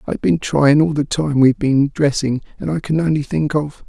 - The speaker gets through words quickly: Yes, fast, 230 wpm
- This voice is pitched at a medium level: Yes, medium, 145 Hz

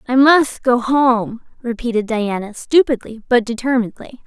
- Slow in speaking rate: Yes, slow, 125 wpm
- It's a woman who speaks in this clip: Yes, female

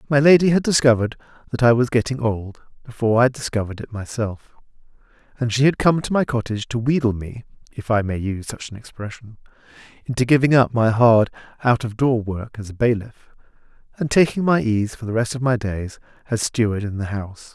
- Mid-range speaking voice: No, low, 120 Hz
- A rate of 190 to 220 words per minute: Yes, average, 200 wpm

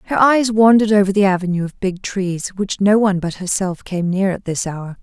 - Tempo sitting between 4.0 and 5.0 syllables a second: No, 5.5 syllables/s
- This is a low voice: No, high, 195 Hz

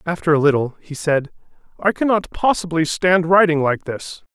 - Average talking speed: Yes, average, 180 wpm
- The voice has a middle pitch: Yes, medium, 165 Hz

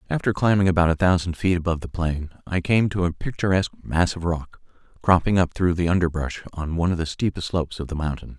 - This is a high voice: No, very low, 85 Hz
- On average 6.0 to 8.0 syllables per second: Yes, 6.3 syllables/s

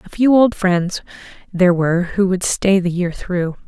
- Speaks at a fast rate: No, average, 195 wpm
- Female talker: Yes, female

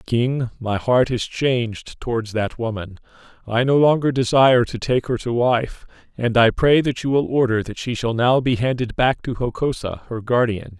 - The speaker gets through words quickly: No, average, 195 wpm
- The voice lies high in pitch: No, low, 120 Hz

